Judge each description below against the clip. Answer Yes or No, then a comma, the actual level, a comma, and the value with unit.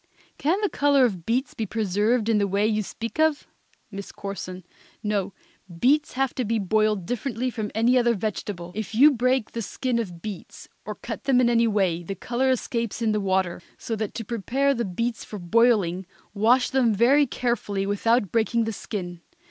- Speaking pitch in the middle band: No, high, 225 Hz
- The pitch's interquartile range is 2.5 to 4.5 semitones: Yes, average, 3.6 semitones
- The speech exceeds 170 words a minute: Yes, average, 190 wpm